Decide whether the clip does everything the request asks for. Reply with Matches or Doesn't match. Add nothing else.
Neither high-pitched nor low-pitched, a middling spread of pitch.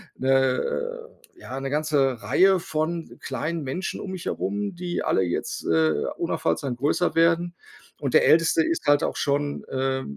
Matches